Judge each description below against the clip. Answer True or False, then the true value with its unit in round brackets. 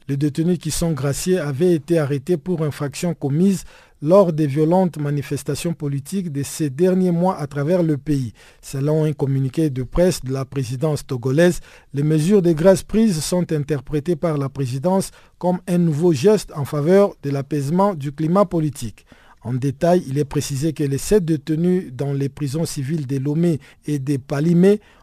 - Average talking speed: True (175 wpm)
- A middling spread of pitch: True (3.7 semitones)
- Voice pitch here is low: False (155 Hz)